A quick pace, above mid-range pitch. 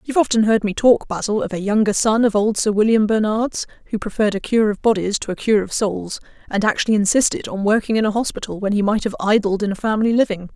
Yes: fast, 245 wpm; high, 215 Hz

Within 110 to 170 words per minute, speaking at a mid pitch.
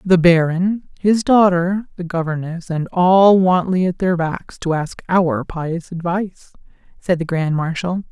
Yes: average, 155 wpm; medium, 175 Hz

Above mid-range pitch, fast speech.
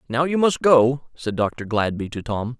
No: low, 125 Hz; fast, 210 wpm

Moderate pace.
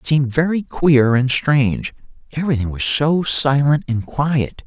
Yes: average, 155 wpm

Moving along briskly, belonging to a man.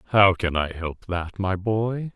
No: average, 195 wpm; male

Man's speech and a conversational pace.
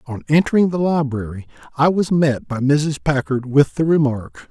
Yes: male; average, 175 wpm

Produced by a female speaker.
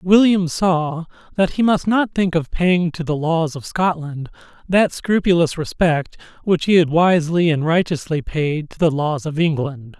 No: male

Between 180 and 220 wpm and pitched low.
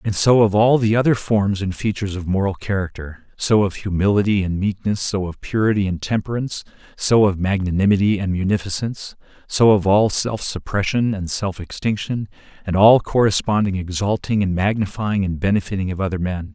No: average, 165 wpm; low, 100 Hz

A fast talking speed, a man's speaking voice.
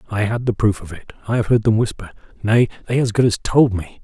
Yes: fast, 270 wpm; male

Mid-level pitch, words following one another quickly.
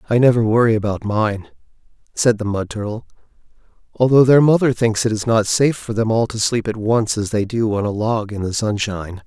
No: low, 110 Hz; fast, 215 wpm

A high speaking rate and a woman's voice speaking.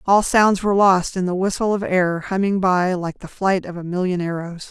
Yes: fast, 230 wpm; female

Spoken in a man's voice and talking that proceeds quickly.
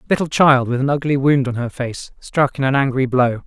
Yes: male; fast, 240 wpm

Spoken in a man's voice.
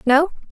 No: female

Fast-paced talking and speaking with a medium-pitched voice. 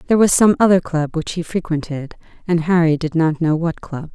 Yes: fast, 215 wpm; medium, 165 Hz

